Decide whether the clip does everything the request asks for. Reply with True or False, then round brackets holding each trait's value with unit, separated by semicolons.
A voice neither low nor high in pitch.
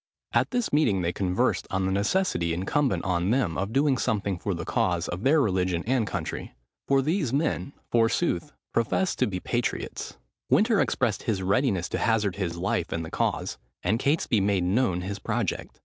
False (105 Hz)